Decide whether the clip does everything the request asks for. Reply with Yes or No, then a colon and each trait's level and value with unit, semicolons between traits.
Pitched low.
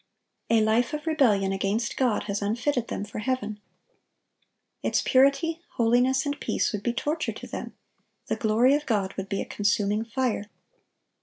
No: high, 230 Hz